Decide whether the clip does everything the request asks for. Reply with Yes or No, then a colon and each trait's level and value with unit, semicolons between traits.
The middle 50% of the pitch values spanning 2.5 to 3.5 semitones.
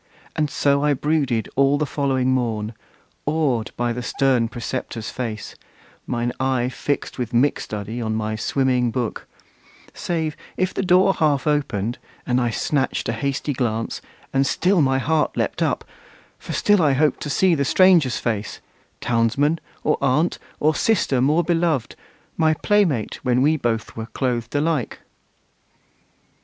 No: average, 4.2 semitones